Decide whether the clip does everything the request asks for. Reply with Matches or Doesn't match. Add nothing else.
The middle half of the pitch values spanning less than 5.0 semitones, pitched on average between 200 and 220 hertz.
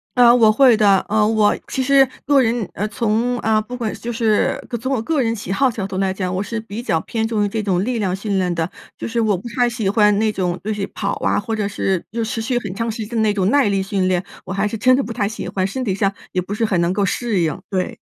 Matches